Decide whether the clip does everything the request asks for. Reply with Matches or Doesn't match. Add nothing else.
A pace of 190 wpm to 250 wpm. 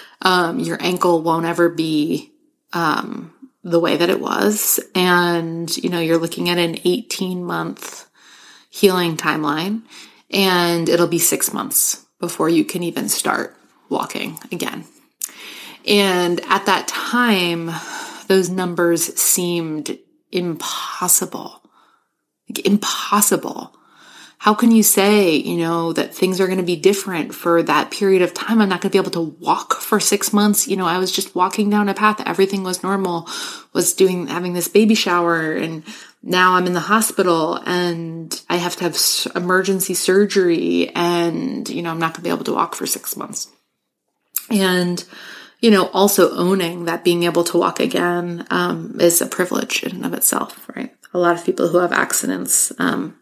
Doesn't match